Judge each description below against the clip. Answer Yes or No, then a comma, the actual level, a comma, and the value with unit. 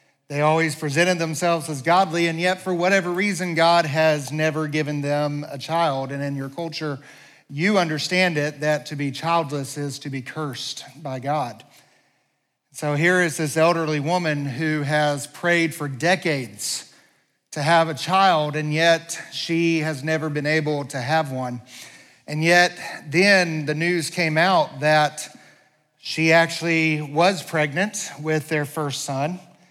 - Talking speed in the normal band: Yes, average, 155 wpm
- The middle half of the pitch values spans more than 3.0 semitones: No, narrow, 2.4 semitones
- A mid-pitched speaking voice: Yes, medium, 155 Hz